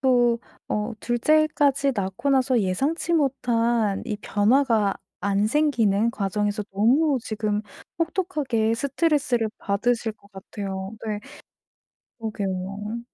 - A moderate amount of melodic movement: Yes, average, 4.6 semitones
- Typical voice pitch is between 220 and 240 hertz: Yes, high, 230 Hz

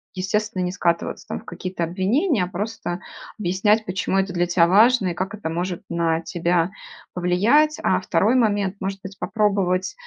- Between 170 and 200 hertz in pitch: Yes, medium, 185 Hz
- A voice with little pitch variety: No, average, 3.0 semitones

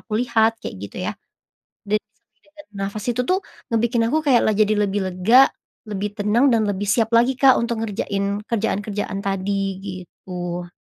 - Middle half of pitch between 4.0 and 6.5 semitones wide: No, average, 2.7 semitones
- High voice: Yes, high, 210 Hz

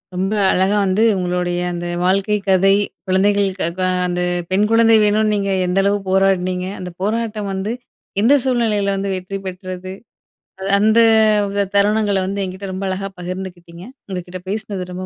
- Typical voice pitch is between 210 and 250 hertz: No, high, 195 Hz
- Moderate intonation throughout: No, narrow, 1.9 semitones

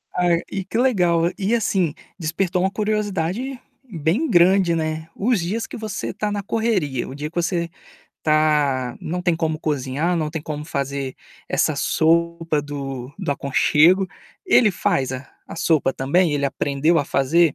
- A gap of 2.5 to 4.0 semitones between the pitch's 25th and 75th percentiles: No, average, 4.5 semitones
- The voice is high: No, medium, 165 Hz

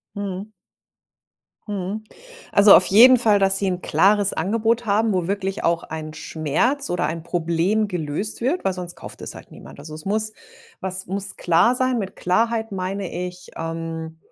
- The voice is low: No, high, 195 Hz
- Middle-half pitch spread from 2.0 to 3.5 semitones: No, average, 4.0 semitones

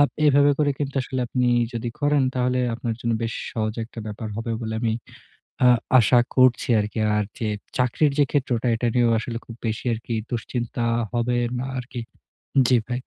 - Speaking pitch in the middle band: No, low, 120 Hz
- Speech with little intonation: Yes, narrow, 1.9 semitones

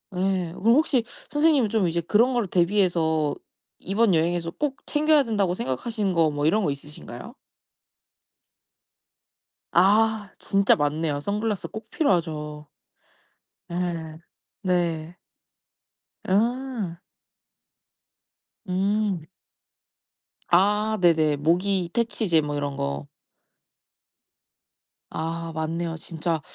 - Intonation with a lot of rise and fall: No, average, 5.0 semitones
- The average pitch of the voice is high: No, medium, 180 Hz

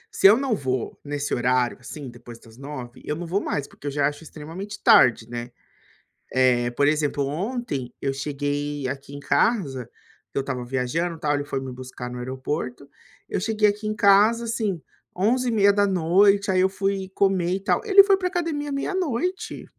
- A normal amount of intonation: No, wide, 7.5 semitones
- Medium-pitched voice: Yes, medium, 150 Hz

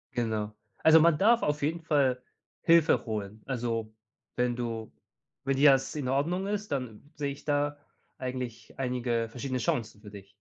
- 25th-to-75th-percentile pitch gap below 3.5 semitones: No, average, 4.3 semitones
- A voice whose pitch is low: Yes, low, 130 Hz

